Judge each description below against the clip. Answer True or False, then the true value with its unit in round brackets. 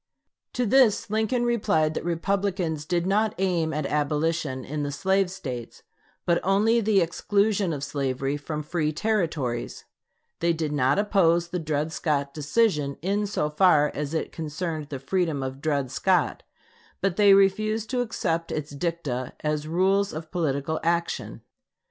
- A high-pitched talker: False (165 Hz)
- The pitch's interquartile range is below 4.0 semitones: False (4.7 semitones)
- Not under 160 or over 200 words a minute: False (150 wpm)